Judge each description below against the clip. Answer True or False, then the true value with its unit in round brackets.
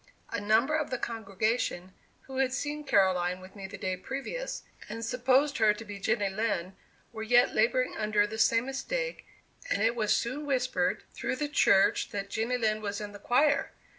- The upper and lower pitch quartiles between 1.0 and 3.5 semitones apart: False (4.4 semitones)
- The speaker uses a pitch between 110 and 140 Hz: False (225 Hz)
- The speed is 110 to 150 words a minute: False (185 wpm)